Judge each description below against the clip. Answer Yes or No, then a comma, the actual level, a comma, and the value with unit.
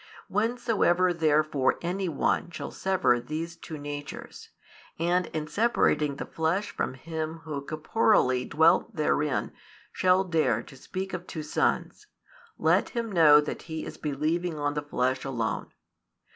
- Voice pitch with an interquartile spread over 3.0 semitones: Yes, average, 3.7 semitones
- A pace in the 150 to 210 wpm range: No, average, 140 wpm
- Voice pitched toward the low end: No, medium, 160 Hz